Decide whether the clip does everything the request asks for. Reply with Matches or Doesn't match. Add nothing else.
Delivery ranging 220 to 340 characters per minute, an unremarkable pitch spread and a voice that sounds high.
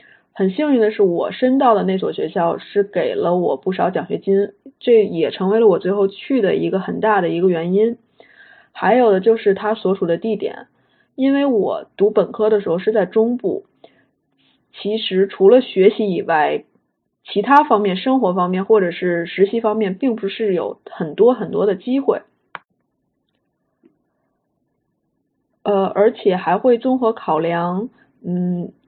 Matches